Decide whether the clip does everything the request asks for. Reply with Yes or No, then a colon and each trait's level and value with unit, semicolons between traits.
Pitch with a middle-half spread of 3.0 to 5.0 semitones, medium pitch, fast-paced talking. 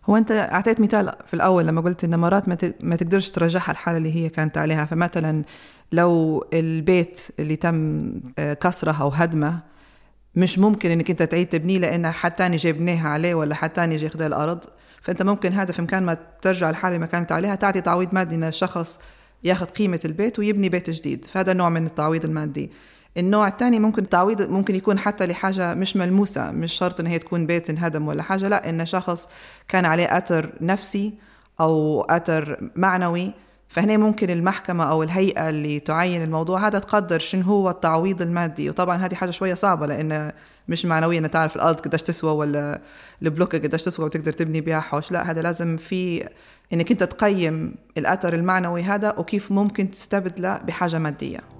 No: narrow, 2.6 semitones; medium, 175 Hz; fast, 175 wpm